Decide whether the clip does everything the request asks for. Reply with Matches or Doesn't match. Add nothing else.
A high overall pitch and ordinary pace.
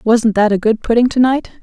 Doesn't match